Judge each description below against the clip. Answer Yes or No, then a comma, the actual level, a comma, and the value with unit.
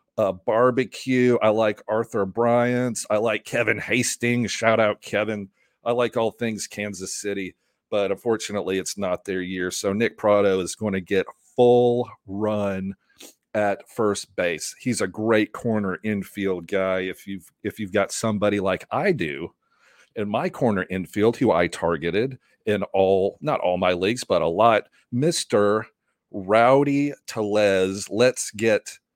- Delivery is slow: No, average, 150 wpm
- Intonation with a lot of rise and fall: No, average, 3.6 semitones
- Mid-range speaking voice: No, low, 105 Hz